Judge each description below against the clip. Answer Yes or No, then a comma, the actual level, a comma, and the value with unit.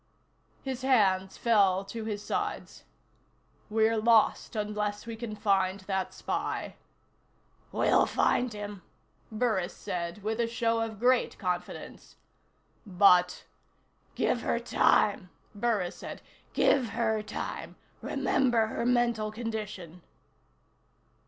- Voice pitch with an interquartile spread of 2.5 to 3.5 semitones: Yes, average, 2.8 semitones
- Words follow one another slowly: Yes, slow, 110 wpm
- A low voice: No, high, 215 Hz